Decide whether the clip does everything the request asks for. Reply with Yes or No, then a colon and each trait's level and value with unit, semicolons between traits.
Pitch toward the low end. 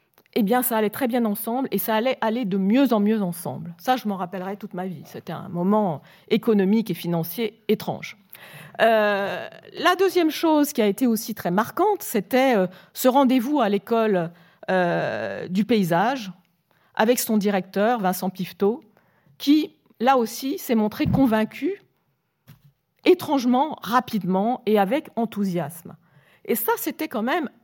No: high, 215 Hz